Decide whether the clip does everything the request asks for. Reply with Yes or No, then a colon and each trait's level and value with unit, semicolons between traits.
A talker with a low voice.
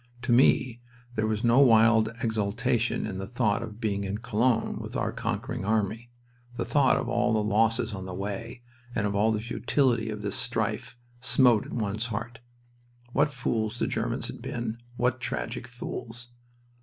Yes: low, 115 Hz